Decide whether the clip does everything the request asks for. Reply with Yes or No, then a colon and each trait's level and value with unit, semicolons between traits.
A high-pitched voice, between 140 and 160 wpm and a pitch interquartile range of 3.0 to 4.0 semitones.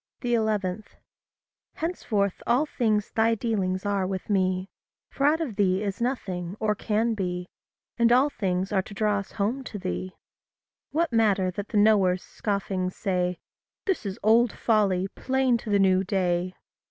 Yes: high, 205 Hz; average, 155 wpm; average, 3.4 semitones